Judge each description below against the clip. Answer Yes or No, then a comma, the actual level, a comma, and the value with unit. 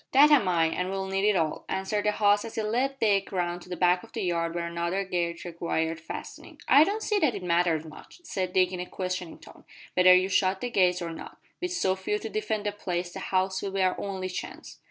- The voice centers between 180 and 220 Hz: Yes, medium, 185 Hz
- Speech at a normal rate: No, fast, 245 wpm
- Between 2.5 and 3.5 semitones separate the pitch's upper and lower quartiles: Yes, average, 2.8 semitones